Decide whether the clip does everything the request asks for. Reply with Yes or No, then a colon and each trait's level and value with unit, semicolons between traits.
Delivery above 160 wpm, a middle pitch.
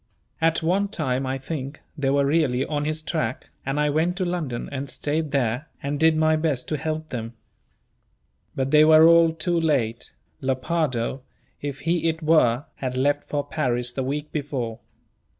Yes: average, 170 wpm; medium, 145 Hz